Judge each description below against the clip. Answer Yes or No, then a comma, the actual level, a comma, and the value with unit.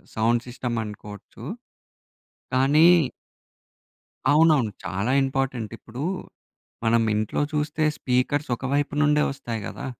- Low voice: Yes, low, 130 Hz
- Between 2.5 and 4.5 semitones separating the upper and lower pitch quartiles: Yes, average, 4.2 semitones